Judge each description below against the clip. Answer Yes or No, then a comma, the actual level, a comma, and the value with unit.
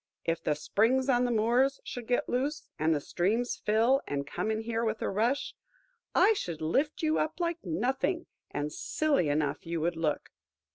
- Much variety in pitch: Yes, wide, 8.3 semitones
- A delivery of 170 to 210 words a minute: Yes, average, 185 wpm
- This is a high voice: Yes, high, 225 Hz